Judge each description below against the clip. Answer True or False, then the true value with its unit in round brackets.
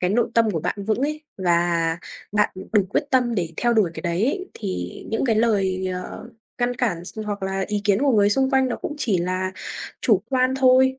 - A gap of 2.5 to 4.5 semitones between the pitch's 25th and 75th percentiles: False (5.1 semitones)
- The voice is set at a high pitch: True (210 Hz)